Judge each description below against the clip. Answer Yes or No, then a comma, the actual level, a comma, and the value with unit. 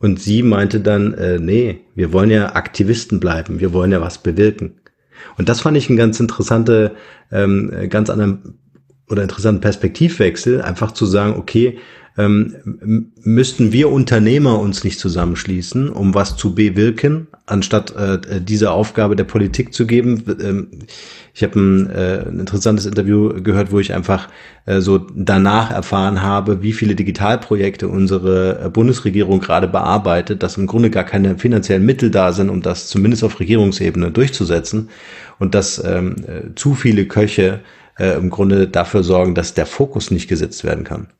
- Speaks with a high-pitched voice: No, low, 105 Hz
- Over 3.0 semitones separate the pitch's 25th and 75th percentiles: No, narrow, 2.6 semitones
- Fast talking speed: No, average, 155 wpm